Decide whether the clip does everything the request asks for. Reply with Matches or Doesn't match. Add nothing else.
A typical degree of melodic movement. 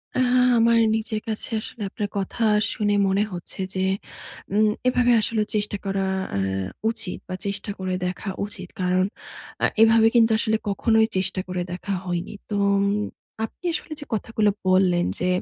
Matches